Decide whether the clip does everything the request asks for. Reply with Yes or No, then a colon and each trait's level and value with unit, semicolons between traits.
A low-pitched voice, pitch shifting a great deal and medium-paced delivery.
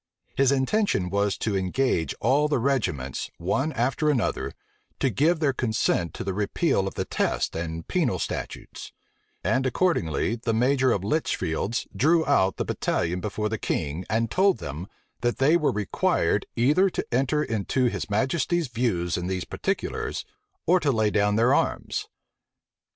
Yes: low, 115 Hz; wide, 6.3 semitones; average, 155 wpm